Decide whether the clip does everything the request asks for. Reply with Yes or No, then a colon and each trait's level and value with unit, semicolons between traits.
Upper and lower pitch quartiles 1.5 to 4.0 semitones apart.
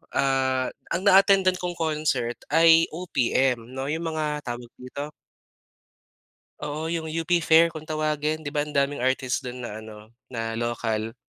No: average, 4.4 semitones